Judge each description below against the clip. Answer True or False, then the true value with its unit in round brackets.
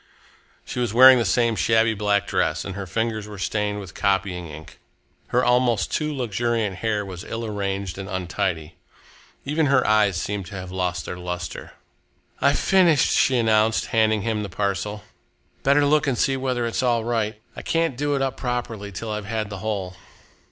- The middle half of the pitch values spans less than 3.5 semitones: False (4.0 semitones)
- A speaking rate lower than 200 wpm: True (180 wpm)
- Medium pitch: False (110 Hz)